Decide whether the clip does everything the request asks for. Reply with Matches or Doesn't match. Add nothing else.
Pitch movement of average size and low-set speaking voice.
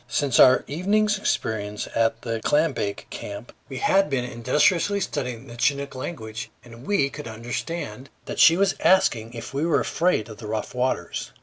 Doesn't match